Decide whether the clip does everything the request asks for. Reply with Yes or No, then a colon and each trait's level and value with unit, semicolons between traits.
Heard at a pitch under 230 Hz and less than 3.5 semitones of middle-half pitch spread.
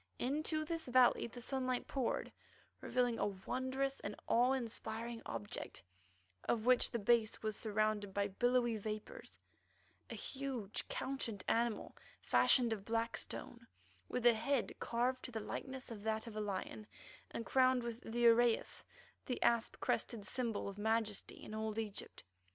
No: high, 235 Hz; average, 2.7 semitones